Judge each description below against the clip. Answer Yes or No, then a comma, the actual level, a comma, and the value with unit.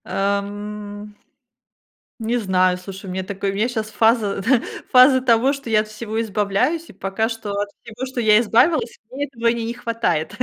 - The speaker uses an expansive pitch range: No, average, 3.0 semitones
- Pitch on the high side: Yes, high, 220 Hz